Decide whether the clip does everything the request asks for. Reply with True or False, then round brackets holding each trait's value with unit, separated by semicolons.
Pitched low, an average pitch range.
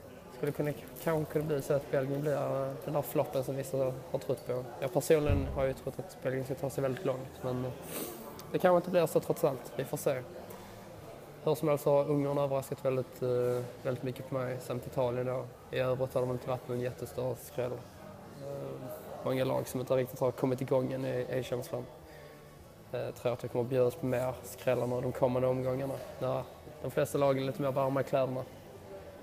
False (130 Hz; 1.8 semitones)